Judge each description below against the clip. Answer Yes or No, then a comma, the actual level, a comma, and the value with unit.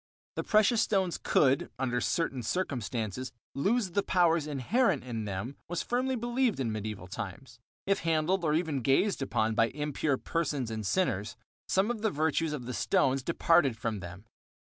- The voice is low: No, medium, 145 Hz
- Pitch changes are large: Yes, wide, 7.8 semitones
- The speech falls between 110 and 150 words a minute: No, average, 160 wpm